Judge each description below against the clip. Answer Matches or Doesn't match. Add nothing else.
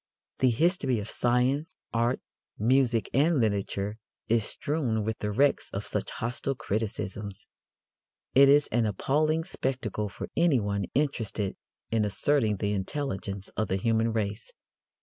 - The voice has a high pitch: Doesn't match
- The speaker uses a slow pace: Matches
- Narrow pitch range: Doesn't match